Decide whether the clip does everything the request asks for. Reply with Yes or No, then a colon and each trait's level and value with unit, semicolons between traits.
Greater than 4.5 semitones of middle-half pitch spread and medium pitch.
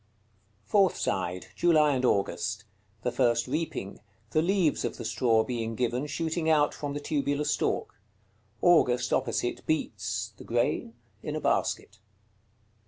No: average, 5.2 semitones; low, 125 Hz